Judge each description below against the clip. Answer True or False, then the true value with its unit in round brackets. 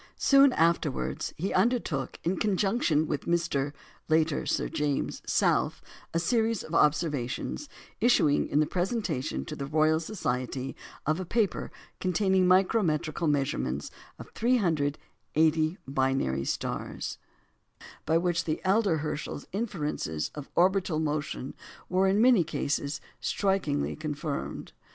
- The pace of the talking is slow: True (120 wpm)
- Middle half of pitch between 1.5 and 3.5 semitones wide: False (4.6 semitones)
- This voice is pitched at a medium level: True (160 Hz)